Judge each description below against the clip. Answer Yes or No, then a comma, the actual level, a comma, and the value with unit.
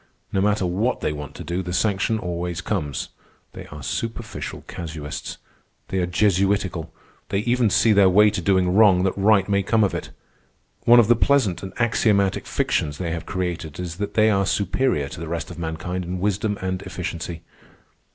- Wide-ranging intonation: No, average, 3.2 semitones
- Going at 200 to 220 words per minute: No, average, 185 wpm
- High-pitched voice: No, very low, 95 Hz